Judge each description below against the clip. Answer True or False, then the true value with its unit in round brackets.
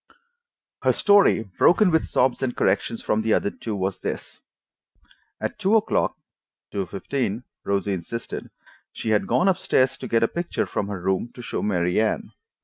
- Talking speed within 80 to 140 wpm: False (170 wpm)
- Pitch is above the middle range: False (110 Hz)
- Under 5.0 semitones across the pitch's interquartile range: False (5.3 semitones)